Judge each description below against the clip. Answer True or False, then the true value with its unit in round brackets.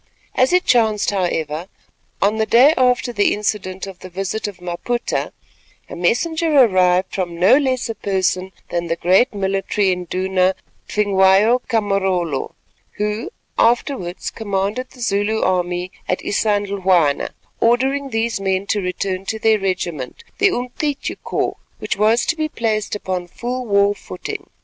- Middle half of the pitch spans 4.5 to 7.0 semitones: False (4.0 semitones)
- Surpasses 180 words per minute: False (145 wpm)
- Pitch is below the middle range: False (200 Hz)